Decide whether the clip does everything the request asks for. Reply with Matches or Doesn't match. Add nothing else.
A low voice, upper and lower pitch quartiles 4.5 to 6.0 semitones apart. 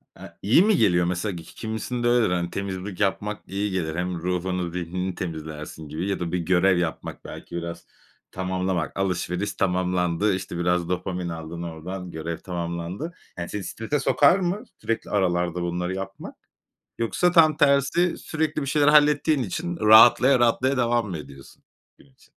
Matches